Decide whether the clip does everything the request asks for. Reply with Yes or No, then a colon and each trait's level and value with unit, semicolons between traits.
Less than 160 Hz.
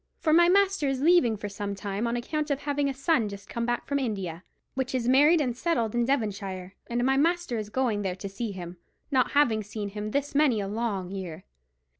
No: high, 235 Hz